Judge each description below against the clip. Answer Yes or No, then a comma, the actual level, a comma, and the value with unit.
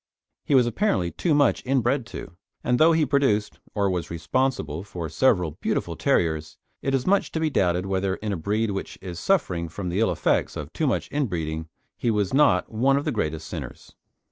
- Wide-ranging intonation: Yes, wide, 7.8 semitones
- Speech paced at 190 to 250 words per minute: Yes, average, 195 wpm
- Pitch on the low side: Yes, low, 105 Hz